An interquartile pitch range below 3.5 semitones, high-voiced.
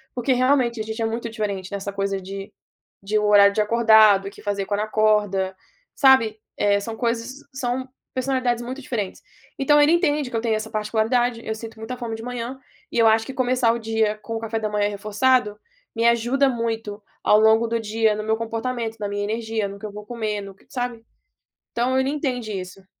Yes: narrow, 2.6 semitones; high, 225 Hz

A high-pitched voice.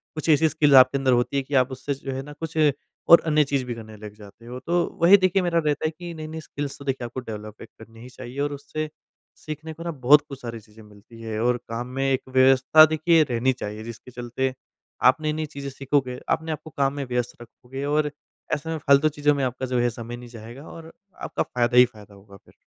No: low, 135 Hz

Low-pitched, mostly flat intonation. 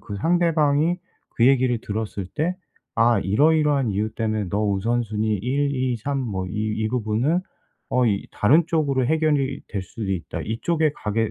No: low, 120 Hz; wide, 5.4 semitones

